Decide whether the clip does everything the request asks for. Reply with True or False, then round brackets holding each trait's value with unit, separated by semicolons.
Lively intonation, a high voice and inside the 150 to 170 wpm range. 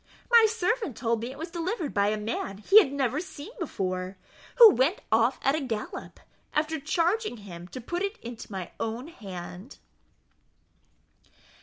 True (8.3 semitones; 265 Hz; 160 wpm)